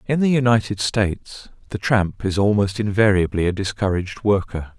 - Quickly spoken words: No, average, 150 wpm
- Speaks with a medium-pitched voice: No, low, 100 Hz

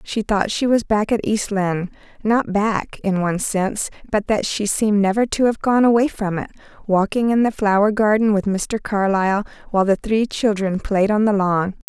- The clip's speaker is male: No, female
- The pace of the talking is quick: No, average, 190 wpm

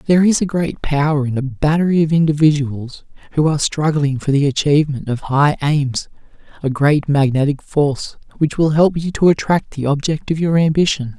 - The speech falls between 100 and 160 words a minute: No, average, 180 wpm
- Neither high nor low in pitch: Yes, medium, 150 Hz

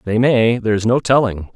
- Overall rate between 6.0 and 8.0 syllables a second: No, 5.6 syllables/s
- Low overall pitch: Yes, low, 115 Hz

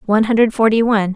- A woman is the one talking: Yes, female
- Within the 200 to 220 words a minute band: Yes, fast, 205 wpm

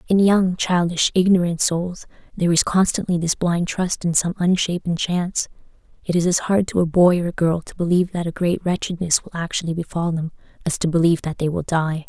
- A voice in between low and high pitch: Yes, medium, 175 Hz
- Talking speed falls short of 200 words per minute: No, fast, 205 wpm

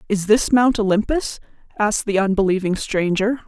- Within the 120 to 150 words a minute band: Yes, average, 140 wpm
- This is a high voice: Yes, high, 210 Hz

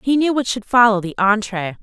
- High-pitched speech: Yes, high, 220 Hz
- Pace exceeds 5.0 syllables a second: Yes, 5.5 syllables/s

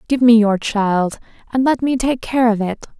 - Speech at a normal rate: No, fast, 220 wpm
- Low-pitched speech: No, high, 230 Hz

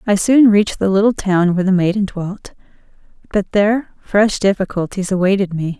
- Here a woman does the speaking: Yes, female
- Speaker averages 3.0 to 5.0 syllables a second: No, 5.5 syllables/s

